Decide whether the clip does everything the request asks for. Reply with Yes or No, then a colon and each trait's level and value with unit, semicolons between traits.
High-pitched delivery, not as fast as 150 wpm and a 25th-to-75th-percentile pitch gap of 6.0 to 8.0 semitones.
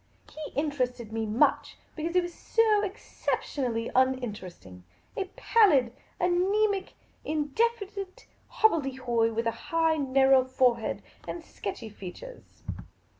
Yes: very high, 280 Hz; average, 140 wpm; wide, 7.7 semitones